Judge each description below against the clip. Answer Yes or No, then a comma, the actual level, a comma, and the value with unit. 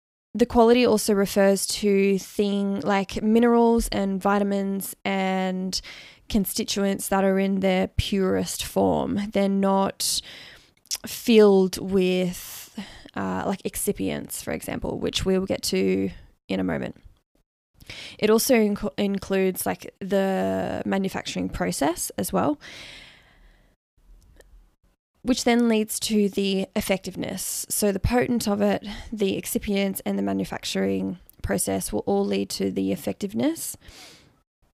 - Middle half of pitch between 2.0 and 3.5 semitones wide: Yes, average, 3.2 semitones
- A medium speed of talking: No, slow, 115 wpm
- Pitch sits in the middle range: No, high, 195 Hz